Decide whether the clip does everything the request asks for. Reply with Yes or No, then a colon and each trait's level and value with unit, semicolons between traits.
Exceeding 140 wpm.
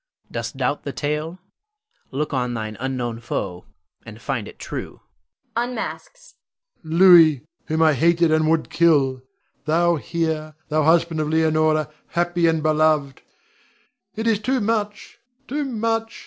No: slow, 135 wpm